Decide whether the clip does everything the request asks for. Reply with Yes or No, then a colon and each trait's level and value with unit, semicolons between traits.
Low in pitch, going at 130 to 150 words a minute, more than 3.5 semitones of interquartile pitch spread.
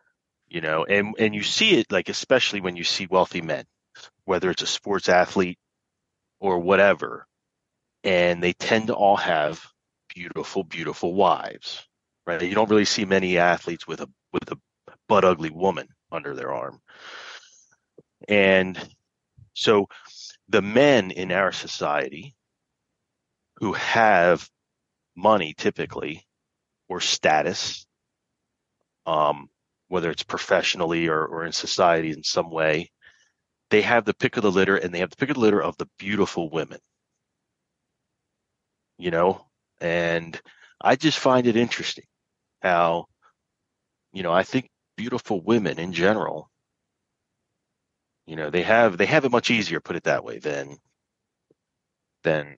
Yes: very low, 95 Hz; average, 140 wpm; average, 4.1 semitones